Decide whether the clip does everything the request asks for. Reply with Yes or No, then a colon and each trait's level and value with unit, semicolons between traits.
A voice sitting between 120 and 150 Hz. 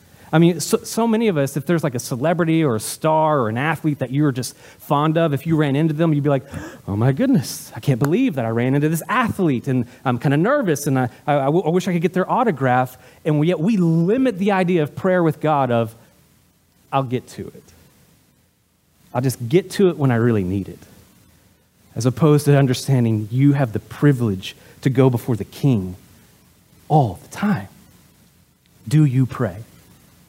Yes: medium, 140 Hz